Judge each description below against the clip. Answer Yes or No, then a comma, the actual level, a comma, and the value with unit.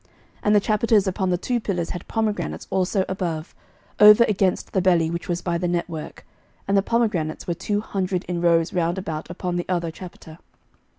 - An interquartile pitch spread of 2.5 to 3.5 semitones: Yes, average, 2.8 semitones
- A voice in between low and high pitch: Yes, medium, 180 Hz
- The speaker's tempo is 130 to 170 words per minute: No, average, 190 wpm